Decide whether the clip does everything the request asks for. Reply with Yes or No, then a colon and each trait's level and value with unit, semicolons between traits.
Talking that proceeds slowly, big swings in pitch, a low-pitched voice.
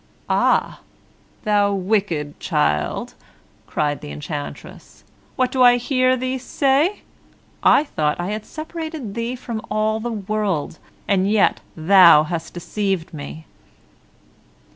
No: slow, 120 wpm; wide, 7.1 semitones; high, 205 Hz